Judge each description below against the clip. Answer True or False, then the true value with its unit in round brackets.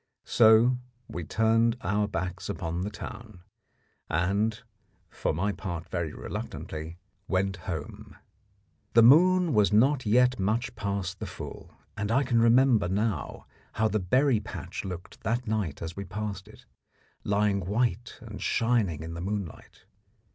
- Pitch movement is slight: False (3.9 semitones)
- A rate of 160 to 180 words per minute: False (140 wpm)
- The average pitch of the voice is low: True (105 Hz)